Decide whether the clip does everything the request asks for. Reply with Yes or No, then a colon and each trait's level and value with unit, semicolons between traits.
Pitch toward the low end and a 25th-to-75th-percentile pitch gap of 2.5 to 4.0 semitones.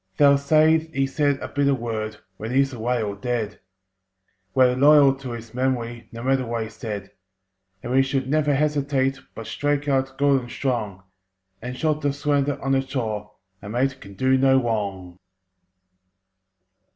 Yes: low, 130 Hz; average, 3.3 semitones